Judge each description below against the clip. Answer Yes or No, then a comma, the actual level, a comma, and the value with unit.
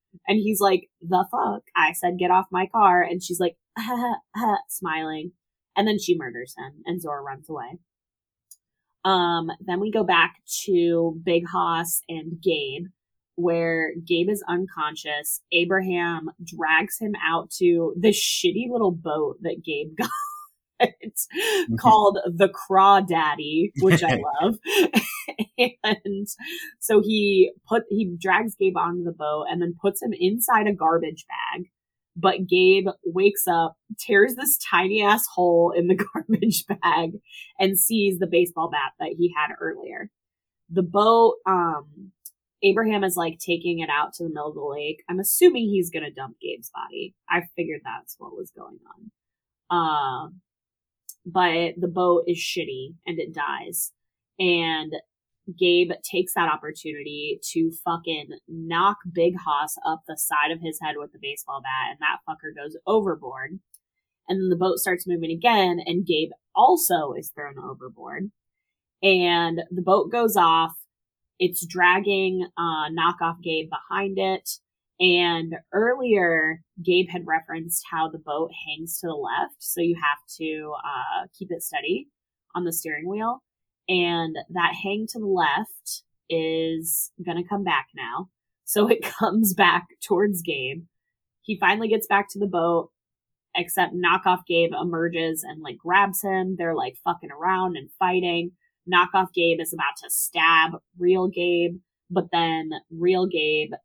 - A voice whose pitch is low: No, medium, 175 Hz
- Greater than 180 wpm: No, average, 150 wpm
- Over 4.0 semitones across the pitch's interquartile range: No, average, 3.2 semitones